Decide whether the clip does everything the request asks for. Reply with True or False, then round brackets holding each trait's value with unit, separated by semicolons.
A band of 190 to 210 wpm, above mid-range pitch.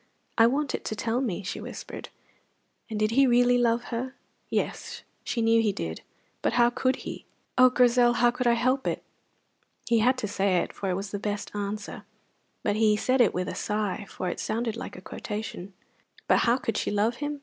True (205 wpm; 230 Hz)